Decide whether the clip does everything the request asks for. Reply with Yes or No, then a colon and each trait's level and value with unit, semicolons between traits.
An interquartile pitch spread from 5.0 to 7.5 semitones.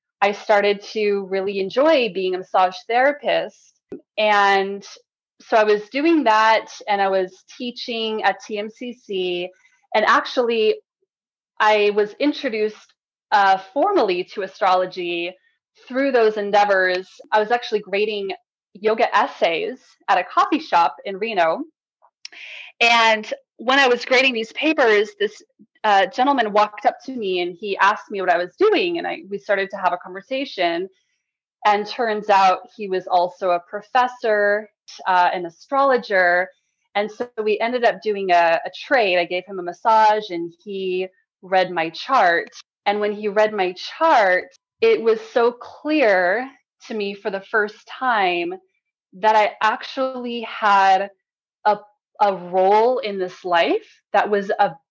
Yes: average, 5.3 semitones